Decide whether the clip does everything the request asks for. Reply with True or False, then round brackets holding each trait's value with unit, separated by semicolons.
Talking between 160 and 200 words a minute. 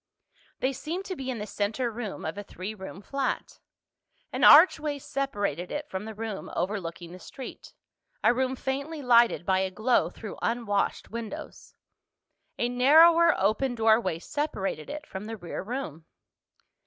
False (150 wpm)